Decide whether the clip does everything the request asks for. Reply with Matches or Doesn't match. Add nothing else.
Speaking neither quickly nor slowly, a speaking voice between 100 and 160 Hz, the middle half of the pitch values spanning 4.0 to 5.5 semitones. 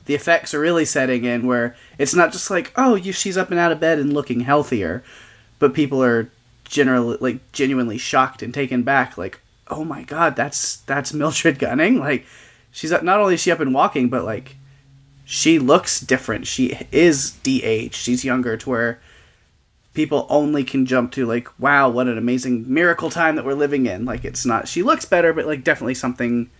Matches